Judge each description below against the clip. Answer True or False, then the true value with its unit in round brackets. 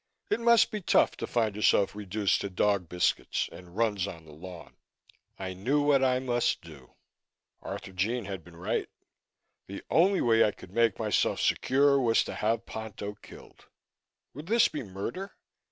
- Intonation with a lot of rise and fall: True (5.8 semitones)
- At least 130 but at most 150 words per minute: False (165 wpm)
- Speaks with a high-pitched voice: False (105 Hz)